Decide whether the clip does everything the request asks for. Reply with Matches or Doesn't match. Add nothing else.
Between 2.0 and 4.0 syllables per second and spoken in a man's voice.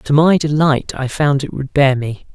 Doesn't match